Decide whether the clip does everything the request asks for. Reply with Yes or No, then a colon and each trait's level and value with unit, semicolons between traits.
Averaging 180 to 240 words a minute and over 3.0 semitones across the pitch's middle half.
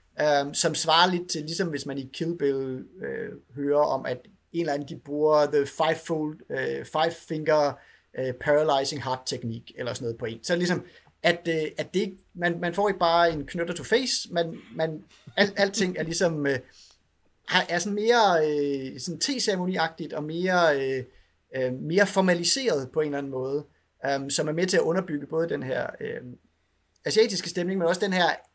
Yes: average, 185 wpm; average, 3.8 semitones